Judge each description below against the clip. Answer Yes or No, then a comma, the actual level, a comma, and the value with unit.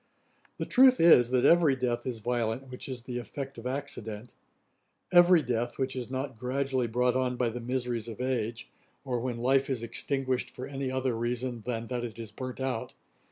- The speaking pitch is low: Yes, low, 125 Hz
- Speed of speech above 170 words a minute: Yes, average, 190 wpm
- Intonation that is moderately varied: No, narrow, 1.9 semitones